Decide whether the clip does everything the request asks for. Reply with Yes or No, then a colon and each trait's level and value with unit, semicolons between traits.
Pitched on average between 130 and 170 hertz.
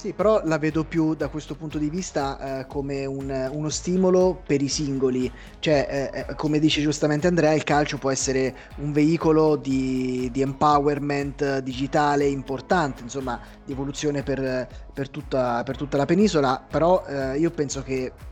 Yes: medium, 140 Hz